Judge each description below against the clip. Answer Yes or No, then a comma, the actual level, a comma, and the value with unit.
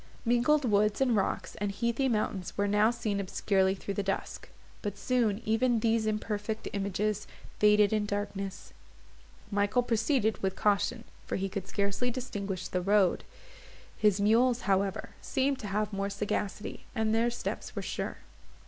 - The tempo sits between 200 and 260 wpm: No, average, 150 wpm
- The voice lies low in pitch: No, high, 210 Hz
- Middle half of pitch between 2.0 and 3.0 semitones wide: Yes, narrow, 2.4 semitones